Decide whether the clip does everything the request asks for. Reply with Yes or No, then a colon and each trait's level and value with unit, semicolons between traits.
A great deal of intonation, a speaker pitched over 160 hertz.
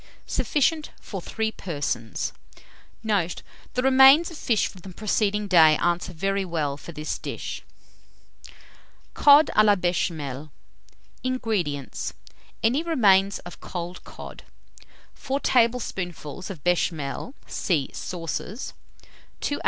Yes: wide, 5.8 semitones; high, 190 Hz